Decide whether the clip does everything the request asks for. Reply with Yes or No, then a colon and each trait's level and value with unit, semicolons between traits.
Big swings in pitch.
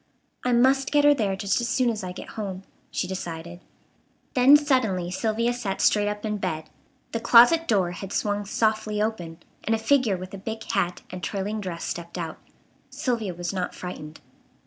No: average, 4.3 semitones